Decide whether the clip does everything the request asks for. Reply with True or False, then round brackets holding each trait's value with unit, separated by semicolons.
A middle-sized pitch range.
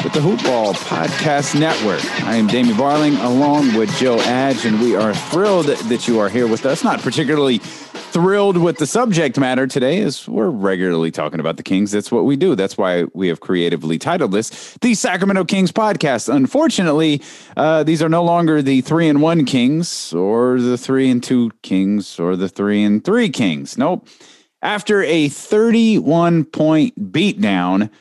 False (7.8 semitones)